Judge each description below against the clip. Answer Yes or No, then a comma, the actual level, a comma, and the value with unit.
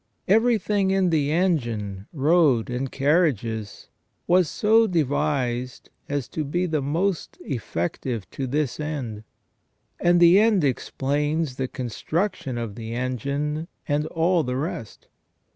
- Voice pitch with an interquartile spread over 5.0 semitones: Yes, wide, 5.5 semitones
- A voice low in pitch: No, medium, 145 Hz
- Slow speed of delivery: Yes, slow, 125 wpm